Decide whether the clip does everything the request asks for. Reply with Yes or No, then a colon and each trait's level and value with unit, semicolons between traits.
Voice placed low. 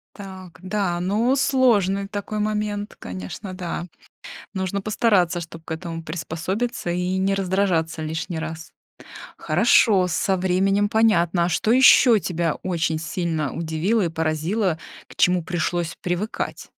No: medium, 185 Hz